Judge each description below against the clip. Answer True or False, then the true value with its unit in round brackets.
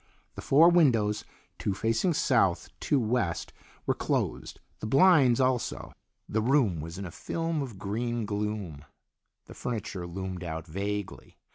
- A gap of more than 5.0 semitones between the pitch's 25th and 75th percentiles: True (5.4 semitones)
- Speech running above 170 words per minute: False (140 wpm)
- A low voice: True (110 Hz)